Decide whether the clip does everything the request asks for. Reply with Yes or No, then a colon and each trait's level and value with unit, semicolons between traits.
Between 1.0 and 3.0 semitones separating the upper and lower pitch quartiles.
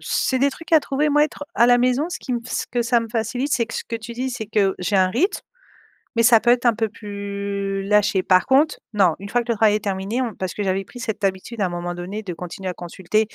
No: average, 3.9 semitones